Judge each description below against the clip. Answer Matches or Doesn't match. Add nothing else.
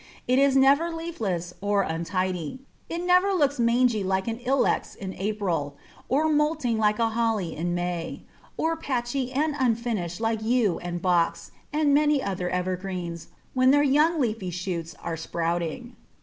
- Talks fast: Doesn't match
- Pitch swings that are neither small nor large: Doesn't match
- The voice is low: Doesn't match